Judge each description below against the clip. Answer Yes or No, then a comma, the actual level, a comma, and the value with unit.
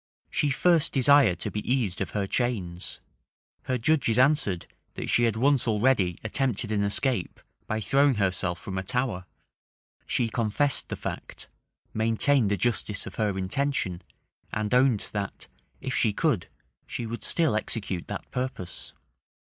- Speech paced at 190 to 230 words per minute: No, average, 150 wpm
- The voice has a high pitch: No, low, 110 Hz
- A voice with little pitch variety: No, average, 4.8 semitones